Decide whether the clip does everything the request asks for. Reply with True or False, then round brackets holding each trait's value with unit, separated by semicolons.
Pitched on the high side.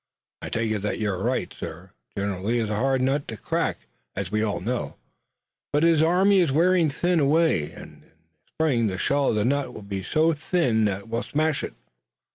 False (125 Hz)